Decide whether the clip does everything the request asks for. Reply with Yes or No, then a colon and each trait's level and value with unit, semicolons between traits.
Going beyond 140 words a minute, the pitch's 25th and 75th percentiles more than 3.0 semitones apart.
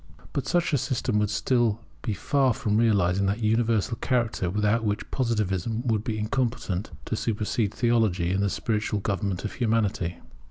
No: average, 160 wpm; narrow, 2.6 semitones